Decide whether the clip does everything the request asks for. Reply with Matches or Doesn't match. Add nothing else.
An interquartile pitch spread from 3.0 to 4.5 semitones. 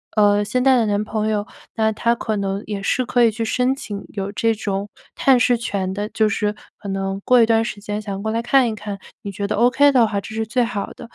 Doesn't match